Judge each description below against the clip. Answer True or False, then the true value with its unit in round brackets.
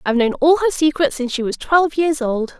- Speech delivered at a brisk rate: True (255 wpm)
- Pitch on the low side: False (285 Hz)